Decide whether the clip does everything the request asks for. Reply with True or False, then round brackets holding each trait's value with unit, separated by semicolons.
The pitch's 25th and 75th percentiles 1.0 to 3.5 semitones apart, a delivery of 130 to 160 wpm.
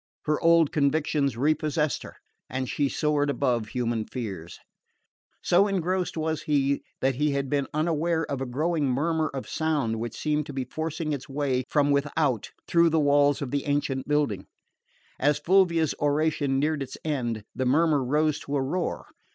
False (2.8 semitones; 170 wpm)